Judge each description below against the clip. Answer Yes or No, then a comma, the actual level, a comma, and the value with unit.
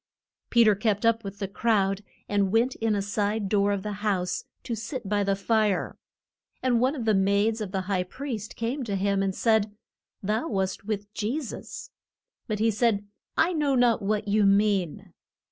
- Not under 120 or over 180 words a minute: No, average, 190 wpm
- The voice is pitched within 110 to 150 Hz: No, high, 210 Hz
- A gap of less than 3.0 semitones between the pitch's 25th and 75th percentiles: Yes, narrow, 2.4 semitones